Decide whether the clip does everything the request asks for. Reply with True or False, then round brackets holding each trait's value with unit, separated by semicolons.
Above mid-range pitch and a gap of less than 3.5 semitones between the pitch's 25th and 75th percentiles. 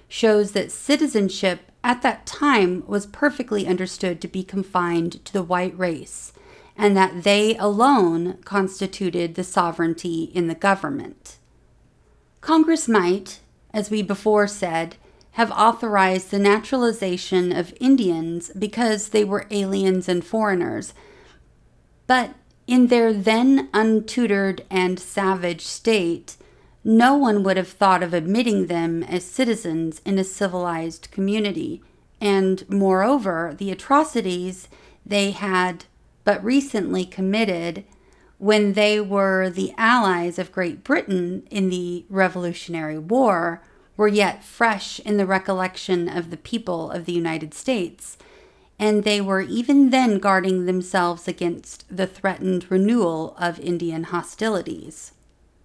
True (195 Hz; 3.0 semitones)